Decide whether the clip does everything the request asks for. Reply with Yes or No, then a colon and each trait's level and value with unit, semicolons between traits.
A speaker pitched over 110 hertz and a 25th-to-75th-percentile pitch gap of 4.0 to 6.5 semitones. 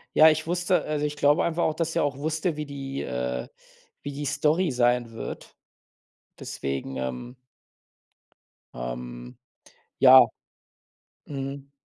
Yes: medium, 140 Hz; wide, 5.5 semitones